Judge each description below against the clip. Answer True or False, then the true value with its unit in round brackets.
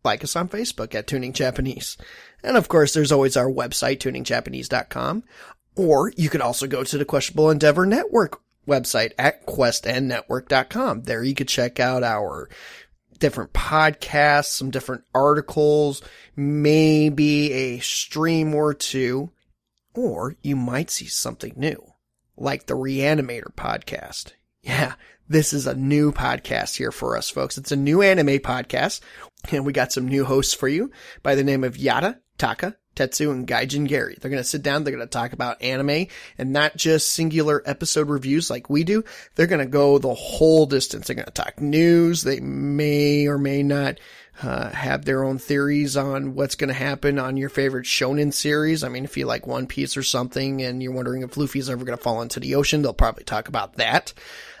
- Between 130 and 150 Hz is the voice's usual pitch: True (140 Hz)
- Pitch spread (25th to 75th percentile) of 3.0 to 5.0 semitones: False (2.4 semitones)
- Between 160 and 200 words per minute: True (175 wpm)